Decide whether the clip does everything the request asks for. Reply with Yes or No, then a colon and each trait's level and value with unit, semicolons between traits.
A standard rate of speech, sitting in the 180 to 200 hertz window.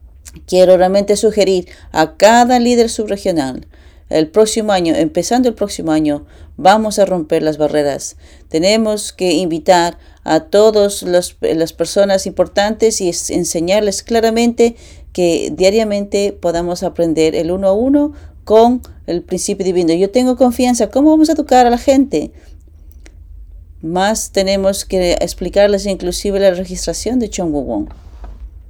No: slow, 130 wpm; high, 190 Hz